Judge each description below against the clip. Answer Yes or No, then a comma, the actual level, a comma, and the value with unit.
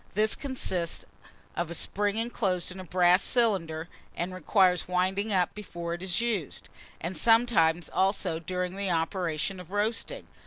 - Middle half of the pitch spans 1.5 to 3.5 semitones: Yes, average, 3.0 semitones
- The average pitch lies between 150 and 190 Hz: Yes, medium, 185 Hz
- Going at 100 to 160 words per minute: Yes, average, 150 wpm